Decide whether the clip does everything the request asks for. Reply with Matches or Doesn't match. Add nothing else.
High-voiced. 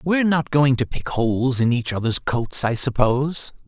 Doesn't match